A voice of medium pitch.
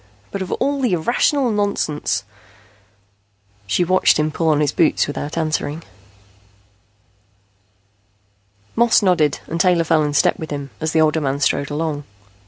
Yes: medium, 155 Hz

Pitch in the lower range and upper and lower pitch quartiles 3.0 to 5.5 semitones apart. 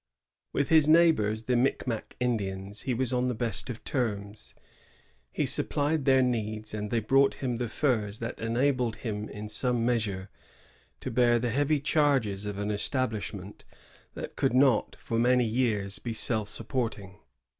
Yes: low, 115 Hz; average, 3.4 semitones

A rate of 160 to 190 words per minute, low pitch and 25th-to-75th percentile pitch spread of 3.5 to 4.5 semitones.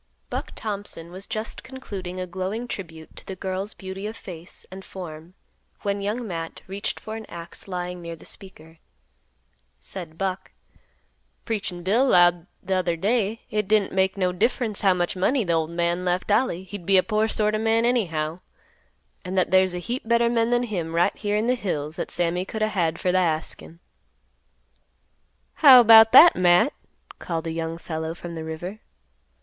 No: average, 180 wpm; high, 190 Hz; average, 3.9 semitones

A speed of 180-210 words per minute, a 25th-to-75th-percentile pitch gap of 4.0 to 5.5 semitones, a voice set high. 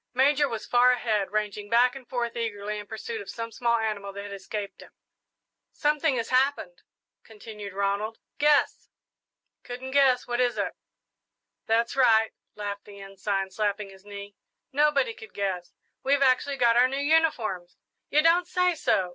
No: average, 160 wpm; average, 5.0 semitones; high, 230 Hz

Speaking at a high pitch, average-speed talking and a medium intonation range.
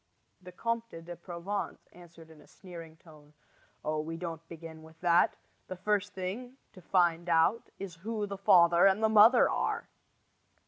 No: medium, 175 Hz; average, 165 wpm; average, 3.5 semitones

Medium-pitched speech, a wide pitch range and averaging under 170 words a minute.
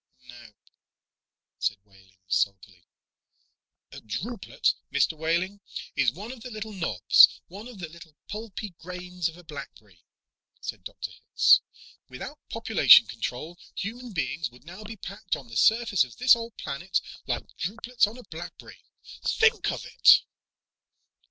Yes: medium, 175 Hz; wide, 8.9 semitones; average, 140 wpm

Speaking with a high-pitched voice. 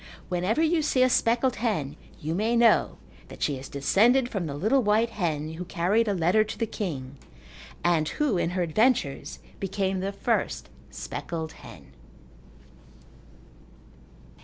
Yes: high, 195 Hz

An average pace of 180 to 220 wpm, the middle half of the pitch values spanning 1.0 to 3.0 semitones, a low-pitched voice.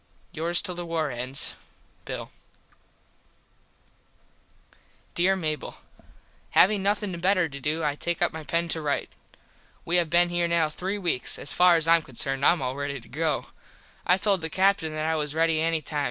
No: average, 185 wpm; narrow, 2.6 semitones; medium, 165 Hz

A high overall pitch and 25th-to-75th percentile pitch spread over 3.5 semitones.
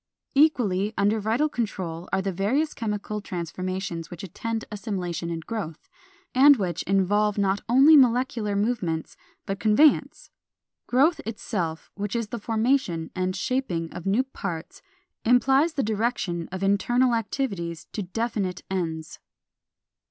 Yes: high, 205 Hz; average, 4.7 semitones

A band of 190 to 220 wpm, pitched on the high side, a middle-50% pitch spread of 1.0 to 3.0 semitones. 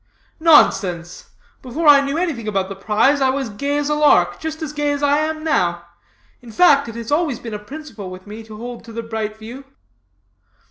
No: fast, 205 wpm; very high, 260 Hz; wide, 5.4 semitones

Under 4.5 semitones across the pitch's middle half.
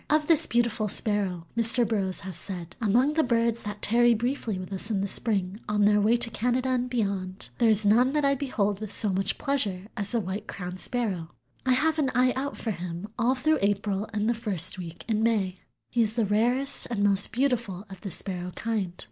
Yes: average, 3.7 semitones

